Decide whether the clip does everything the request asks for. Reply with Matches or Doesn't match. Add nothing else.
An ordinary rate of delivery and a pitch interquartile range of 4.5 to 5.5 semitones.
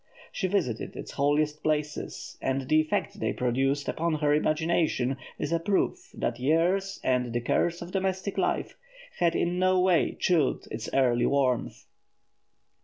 Matches